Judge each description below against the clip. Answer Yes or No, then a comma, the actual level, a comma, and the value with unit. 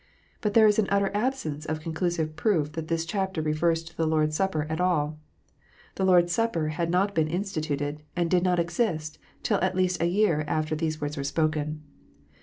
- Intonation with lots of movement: No, average, 3.2 semitones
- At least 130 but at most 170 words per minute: No, fast, 205 wpm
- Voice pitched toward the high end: No, medium, 165 Hz